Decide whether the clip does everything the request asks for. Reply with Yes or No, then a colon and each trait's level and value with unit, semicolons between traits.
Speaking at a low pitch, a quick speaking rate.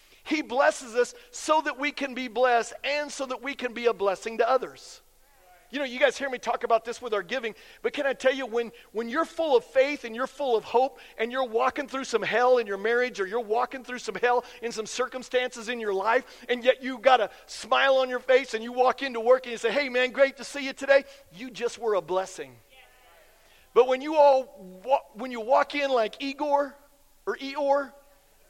No: very high, 255 Hz; fast, 230 wpm